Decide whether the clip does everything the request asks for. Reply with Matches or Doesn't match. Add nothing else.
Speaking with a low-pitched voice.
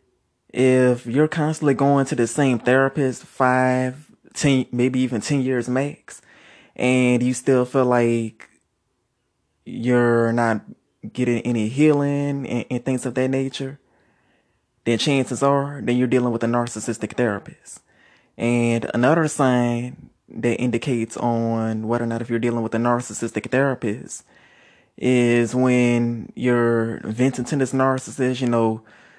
Matches